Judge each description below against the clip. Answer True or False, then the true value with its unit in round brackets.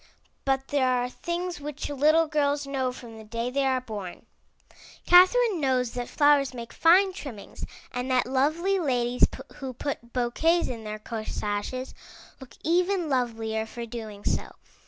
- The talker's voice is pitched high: True (260 Hz)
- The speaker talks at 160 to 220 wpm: False (150 wpm)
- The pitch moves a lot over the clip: False (4.2 semitones)